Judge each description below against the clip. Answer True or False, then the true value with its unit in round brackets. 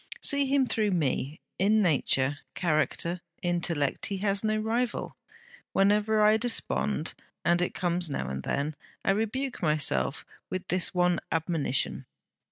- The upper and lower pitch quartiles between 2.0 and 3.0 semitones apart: False (5.5 semitones)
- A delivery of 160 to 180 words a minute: False (135 wpm)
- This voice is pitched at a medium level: True (180 Hz)